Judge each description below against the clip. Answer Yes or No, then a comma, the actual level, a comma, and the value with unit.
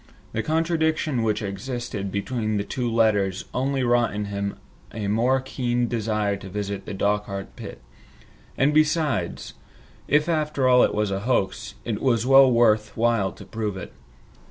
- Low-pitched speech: Yes, low, 115 Hz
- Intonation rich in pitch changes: No, average, 4.3 semitones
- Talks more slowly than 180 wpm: Yes, average, 155 wpm